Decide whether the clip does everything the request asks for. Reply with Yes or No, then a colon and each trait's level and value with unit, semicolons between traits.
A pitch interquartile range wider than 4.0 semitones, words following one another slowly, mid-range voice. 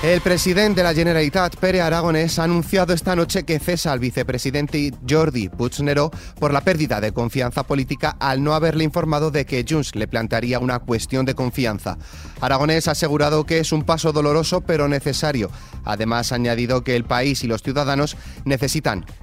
No: average, 4.6 semitones; average, 175 wpm; medium, 145 Hz